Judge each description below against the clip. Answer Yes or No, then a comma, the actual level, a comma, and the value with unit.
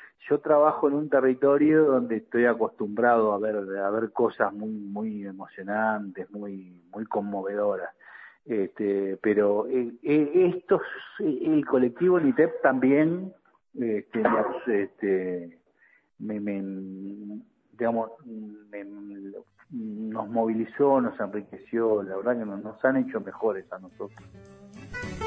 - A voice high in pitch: No, low, 110 Hz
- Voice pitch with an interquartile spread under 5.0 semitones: Yes, average, 4.5 semitones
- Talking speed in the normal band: No, slow, 110 wpm